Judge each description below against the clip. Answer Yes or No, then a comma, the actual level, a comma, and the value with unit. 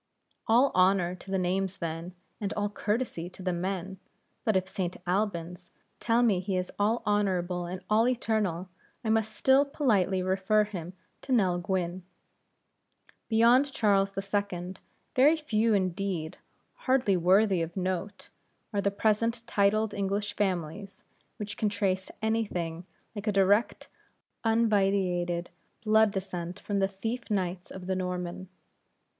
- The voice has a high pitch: Yes, high, 195 Hz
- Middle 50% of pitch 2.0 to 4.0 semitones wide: Yes, average, 2.9 semitones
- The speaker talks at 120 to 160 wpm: Yes, average, 140 wpm